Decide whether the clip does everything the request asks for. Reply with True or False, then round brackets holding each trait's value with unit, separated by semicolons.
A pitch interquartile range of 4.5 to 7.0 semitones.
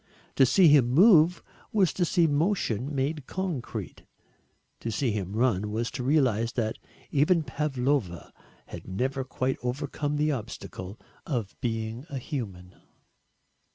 True (4.9 semitones)